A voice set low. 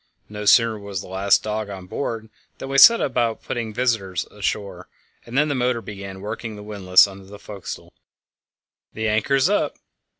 Yes: low, 105 Hz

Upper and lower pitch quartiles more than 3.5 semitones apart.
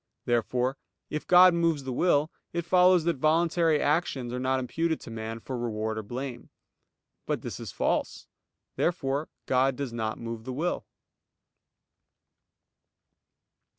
Yes: wide, 5.4 semitones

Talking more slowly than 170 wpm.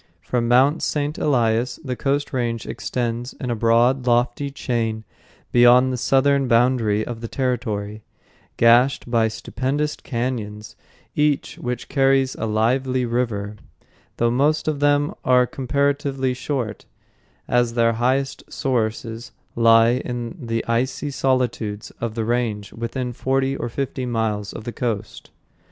Yes: slow, 135 wpm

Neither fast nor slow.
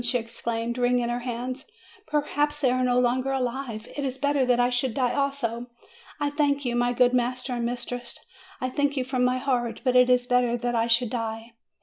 No: fast, 210 wpm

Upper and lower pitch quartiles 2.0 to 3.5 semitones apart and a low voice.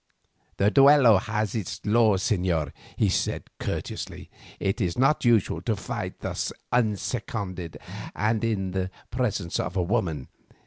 No: average, 4.0 semitones; low, 105 Hz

